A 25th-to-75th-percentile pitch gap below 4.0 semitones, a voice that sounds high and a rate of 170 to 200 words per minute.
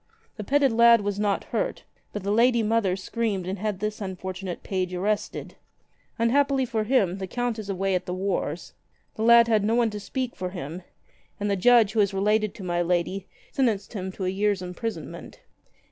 Yes: average, 3.4 semitones; high, 205 Hz; average, 195 wpm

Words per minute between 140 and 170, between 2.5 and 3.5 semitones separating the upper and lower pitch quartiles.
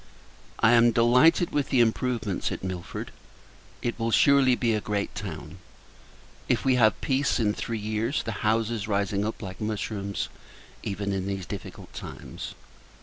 Yes: average, 150 wpm; average, 3.0 semitones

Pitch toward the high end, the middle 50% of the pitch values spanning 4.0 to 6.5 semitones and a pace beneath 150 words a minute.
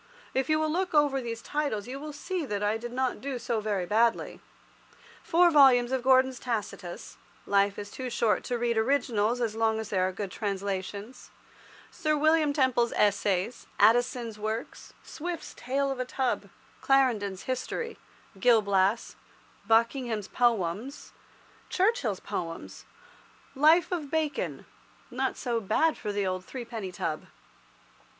Yes: high, 240 Hz; average, 4.7 semitones; average, 140 wpm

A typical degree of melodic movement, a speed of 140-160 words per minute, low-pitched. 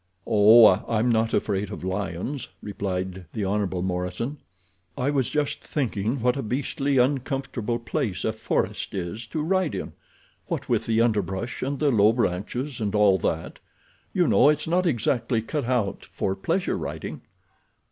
Yes: average, 5.0 semitones; average, 155 wpm; low, 115 Hz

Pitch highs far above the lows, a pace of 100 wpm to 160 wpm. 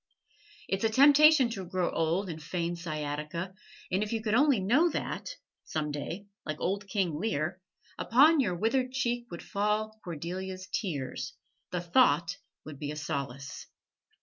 Yes: wide, 5.9 semitones; average, 150 wpm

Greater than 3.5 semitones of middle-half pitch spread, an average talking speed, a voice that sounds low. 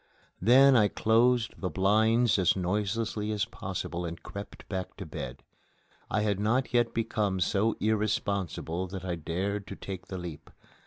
No: average, 2.9 semitones; average, 155 wpm; low, 100 Hz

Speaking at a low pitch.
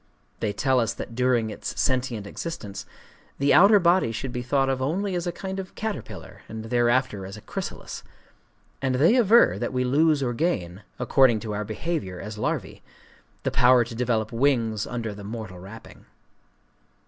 Yes: low, 125 Hz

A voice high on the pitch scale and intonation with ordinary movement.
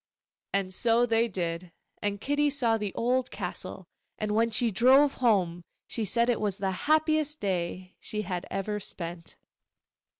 Yes: high, 215 Hz; average, 4.5 semitones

